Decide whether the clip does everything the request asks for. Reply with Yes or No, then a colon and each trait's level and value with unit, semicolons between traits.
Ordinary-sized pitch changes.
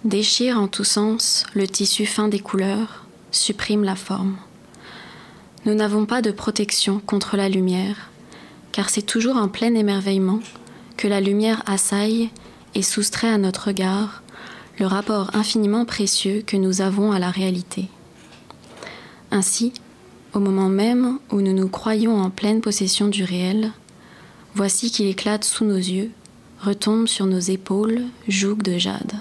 No: narrow, 2.0 semitones